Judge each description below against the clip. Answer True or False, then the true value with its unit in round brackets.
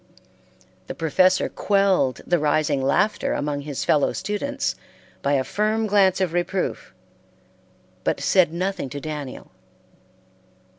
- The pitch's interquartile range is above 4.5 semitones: True (5.3 semitones)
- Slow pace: True (115 wpm)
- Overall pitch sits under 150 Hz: False (175 Hz)